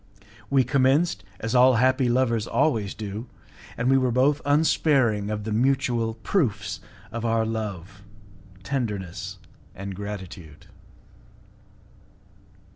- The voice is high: No, low, 115 Hz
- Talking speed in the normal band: No, slow, 110 wpm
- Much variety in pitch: No, average, 4.2 semitones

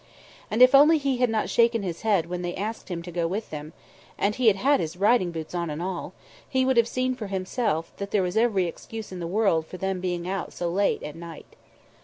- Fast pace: Yes, fast, 245 wpm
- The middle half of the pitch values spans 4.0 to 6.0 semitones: Yes, average, 4.8 semitones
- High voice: Yes, high, 195 Hz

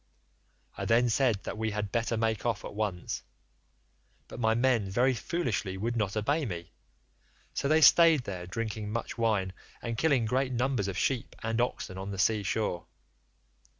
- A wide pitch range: No, average, 3.4 semitones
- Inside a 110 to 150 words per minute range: No, average, 170 wpm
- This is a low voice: Yes, low, 110 Hz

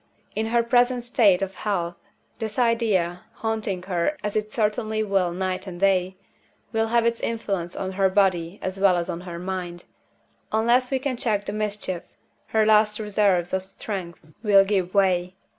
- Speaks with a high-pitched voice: Yes, high, 200 Hz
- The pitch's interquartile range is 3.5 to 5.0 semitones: No, average, 3.1 semitones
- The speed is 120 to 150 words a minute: No, average, 170 wpm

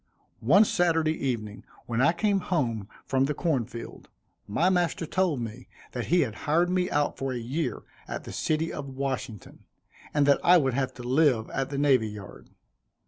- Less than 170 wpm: No, average, 185 wpm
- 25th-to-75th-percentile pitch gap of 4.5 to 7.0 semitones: Yes, average, 5.1 semitones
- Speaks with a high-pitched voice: No, medium, 140 Hz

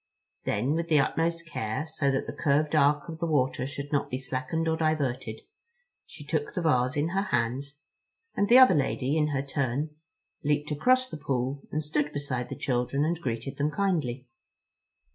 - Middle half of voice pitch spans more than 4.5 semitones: No, average, 3.4 semitones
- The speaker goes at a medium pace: Yes, average, 180 wpm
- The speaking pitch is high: No, medium, 145 Hz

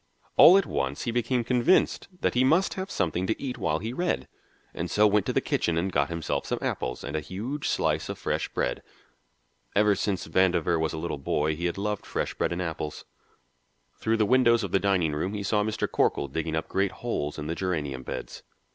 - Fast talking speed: Yes, fast, 215 wpm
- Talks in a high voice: No, very low, 95 Hz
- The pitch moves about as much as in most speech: No, wide, 5.8 semitones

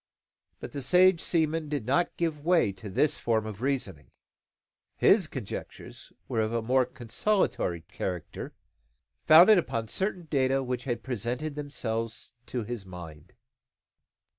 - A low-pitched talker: Yes, low, 125 Hz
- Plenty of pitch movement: Yes, wide, 5.9 semitones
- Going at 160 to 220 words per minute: No, slow, 135 wpm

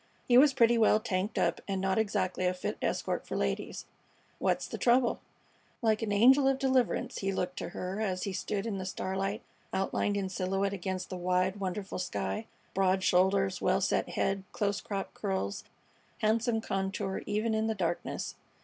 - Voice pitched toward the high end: Yes, high, 195 Hz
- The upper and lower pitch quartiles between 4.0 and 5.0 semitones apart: No, average, 2.7 semitones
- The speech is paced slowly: No, average, 175 wpm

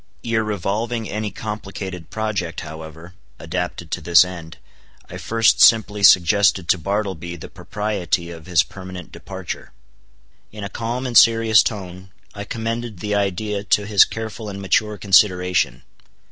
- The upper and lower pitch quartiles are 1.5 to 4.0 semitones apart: Yes, average, 3.5 semitones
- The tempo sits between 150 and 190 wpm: No, average, 140 wpm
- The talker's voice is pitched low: Yes, low, 100 Hz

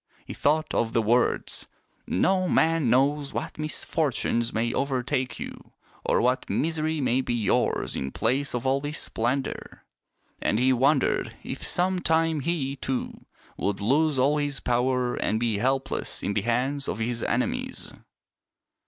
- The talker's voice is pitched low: Yes, low, 130 Hz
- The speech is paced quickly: No, average, 155 wpm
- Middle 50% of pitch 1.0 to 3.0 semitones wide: No, average, 3.8 semitones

